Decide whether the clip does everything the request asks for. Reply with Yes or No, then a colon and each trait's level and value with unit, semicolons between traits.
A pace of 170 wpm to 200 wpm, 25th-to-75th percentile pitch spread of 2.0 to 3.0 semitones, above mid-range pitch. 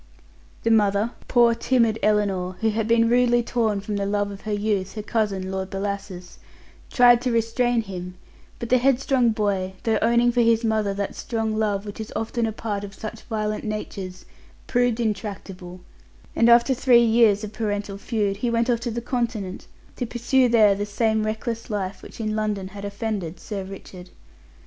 Yes: average, 180 wpm; narrow, 2.6 semitones; high, 215 Hz